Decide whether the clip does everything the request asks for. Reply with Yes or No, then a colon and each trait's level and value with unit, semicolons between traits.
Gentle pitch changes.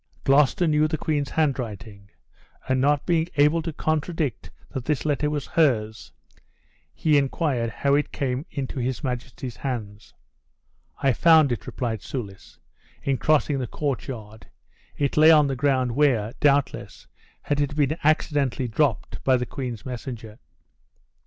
No: average, 3.4 semitones